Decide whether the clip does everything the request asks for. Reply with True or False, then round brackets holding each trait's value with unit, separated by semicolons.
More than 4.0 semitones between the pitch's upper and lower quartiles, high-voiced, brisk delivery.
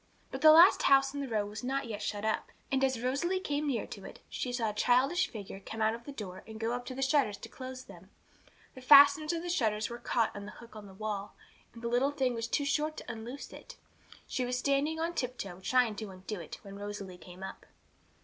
True (4.6 semitones; 245 Hz; 245 wpm)